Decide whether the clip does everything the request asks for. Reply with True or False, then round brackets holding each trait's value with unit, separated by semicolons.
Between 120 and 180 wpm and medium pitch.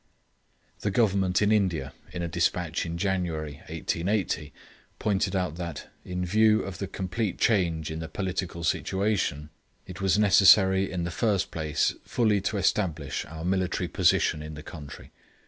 False (150 wpm; 90 Hz)